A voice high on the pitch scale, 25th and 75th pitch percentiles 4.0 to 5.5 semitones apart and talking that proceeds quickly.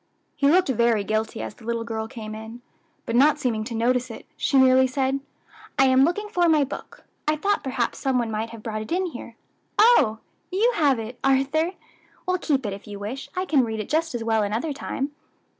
Yes: very high, 260 Hz; average, 5.2 semitones; fast, 215 wpm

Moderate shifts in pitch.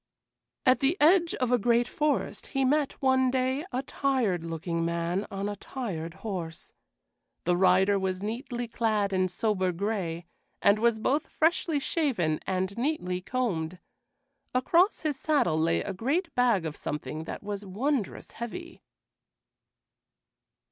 No: wide, 6.4 semitones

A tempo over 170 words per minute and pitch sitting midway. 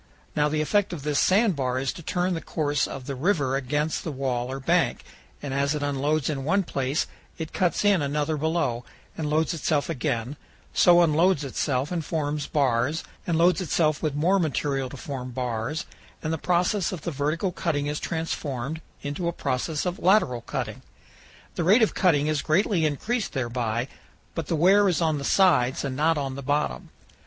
Yes: average, 190 wpm; medium, 150 Hz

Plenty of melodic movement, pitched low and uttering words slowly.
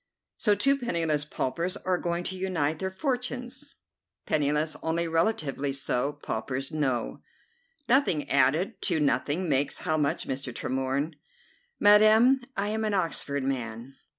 No: wide, 6.6 semitones; medium, 160 Hz; slow, 130 wpm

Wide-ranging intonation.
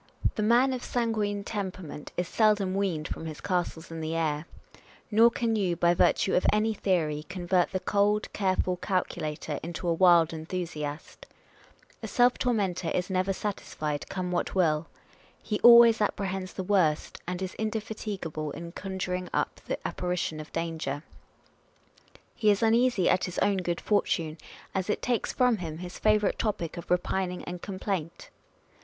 No: average, 3.8 semitones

